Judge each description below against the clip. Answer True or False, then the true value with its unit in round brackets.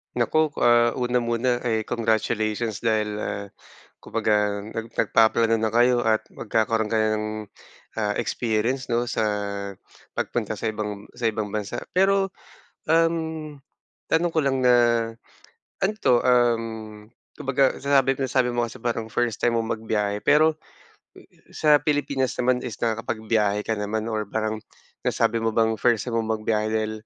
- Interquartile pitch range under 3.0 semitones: True (2.5 semitones)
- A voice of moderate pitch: False (115 Hz)